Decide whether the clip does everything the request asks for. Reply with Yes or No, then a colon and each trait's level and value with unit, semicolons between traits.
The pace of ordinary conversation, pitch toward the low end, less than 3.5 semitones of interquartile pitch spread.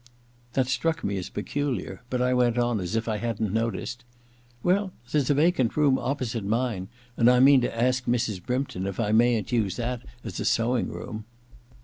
Yes: average, 190 wpm; low, 120 Hz; average, 2.9 semitones